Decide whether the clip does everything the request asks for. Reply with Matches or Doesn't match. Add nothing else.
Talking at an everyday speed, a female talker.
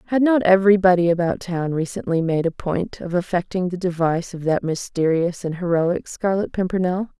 Matches